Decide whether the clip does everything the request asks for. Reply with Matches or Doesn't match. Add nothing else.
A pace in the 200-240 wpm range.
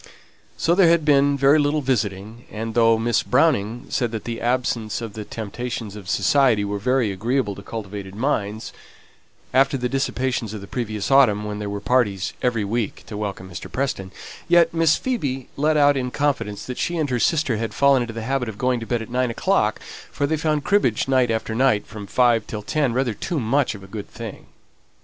Matches